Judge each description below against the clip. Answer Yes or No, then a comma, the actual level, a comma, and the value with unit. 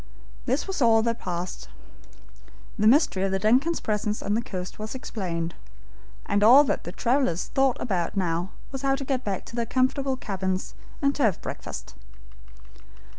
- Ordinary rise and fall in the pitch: No, wide, 5.7 semitones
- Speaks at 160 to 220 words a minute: Yes, average, 165 wpm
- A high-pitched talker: Yes, high, 220 Hz